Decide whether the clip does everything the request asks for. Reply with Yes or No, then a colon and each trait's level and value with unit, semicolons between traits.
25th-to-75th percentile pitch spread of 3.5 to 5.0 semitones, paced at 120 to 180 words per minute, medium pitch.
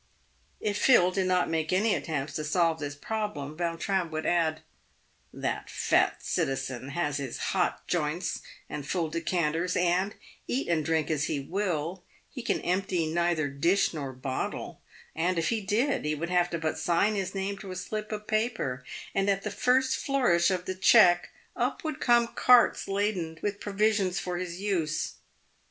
Yes: average, 4.2 semitones; average, 175 wpm; medium, 175 Hz